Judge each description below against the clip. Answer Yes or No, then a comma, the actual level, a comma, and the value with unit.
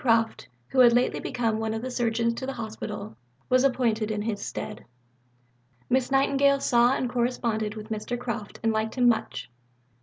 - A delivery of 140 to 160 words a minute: No, average, 175 wpm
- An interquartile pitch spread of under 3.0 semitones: Yes, narrow, 2.4 semitones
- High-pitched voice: Yes, high, 235 Hz